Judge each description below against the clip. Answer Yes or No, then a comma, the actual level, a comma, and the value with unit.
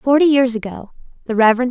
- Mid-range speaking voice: No, high, 245 Hz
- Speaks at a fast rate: No, average, 175 wpm